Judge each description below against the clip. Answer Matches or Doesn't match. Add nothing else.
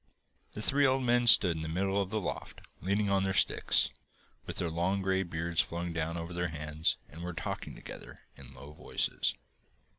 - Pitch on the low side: Matches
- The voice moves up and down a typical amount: Matches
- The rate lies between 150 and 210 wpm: Matches